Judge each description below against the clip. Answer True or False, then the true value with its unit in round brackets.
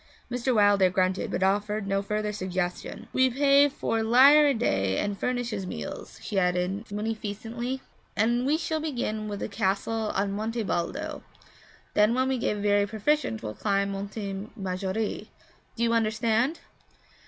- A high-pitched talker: True (215 Hz)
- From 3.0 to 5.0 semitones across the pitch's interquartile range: True (3.3 semitones)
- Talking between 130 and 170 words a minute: True (155 wpm)